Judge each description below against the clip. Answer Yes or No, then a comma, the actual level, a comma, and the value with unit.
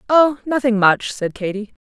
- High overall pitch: Yes, high, 230 Hz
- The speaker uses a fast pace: No, average, 165 wpm